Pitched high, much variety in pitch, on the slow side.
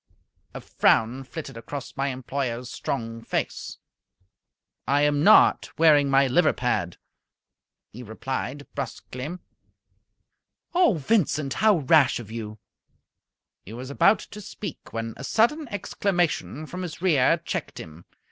No: medium, 140 Hz; wide, 5.8 semitones; slow, 125 wpm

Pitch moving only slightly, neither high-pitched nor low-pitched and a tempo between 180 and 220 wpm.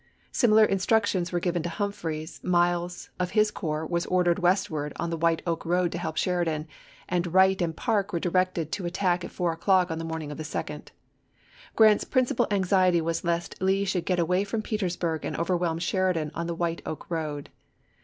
Yes: narrow, 2.2 semitones; medium, 175 Hz; average, 195 wpm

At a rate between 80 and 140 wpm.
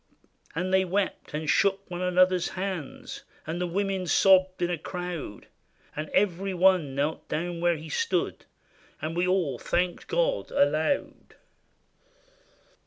Yes: slow, 135 wpm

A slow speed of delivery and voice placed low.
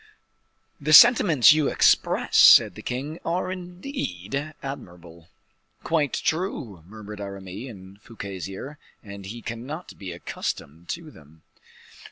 Yes: slow, 120 wpm; low, 115 Hz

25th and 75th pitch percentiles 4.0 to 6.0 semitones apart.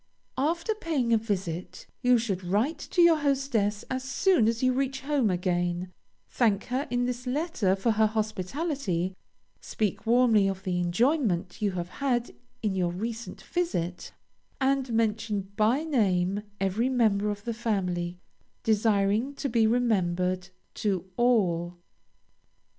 Yes: average, 5.2 semitones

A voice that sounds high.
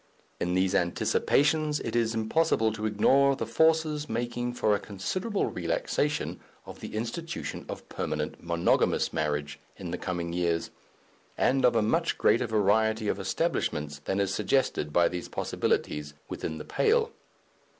No: low, 110 Hz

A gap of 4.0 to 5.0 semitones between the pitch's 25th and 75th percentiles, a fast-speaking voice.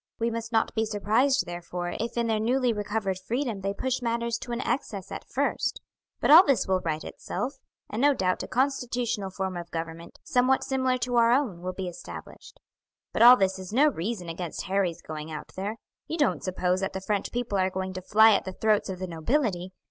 Yes: average, 4.7 semitones; fast, 210 wpm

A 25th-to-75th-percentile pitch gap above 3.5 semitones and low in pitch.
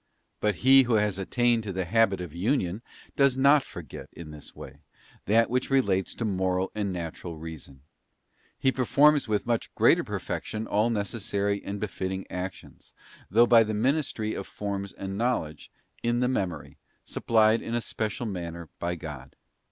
Yes: average, 4.4 semitones; low, 105 Hz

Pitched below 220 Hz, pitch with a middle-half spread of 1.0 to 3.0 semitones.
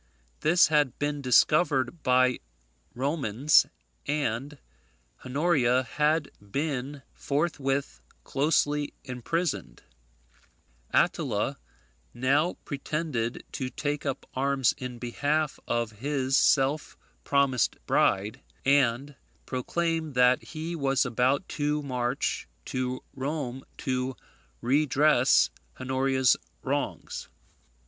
Yes: low, 135 Hz; average, 2.7 semitones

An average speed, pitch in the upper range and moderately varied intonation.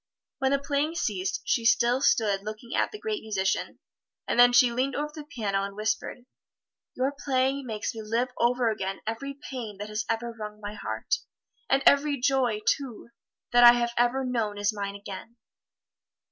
Yes: average, 175 wpm; high, 235 Hz; average, 4.0 semitones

